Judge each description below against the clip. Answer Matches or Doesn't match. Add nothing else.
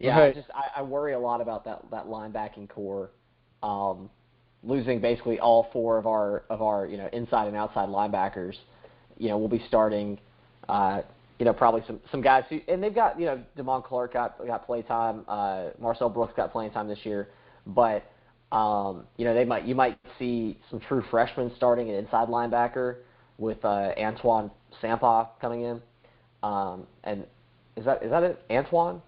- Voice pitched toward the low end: Matches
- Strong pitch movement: Doesn't match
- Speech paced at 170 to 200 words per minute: Matches